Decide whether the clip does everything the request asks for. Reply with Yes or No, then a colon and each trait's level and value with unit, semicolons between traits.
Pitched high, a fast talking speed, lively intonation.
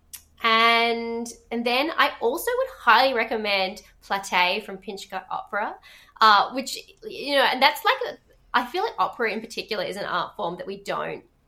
No: high, 230 Hz; average, 175 wpm; wide, 6.4 semitones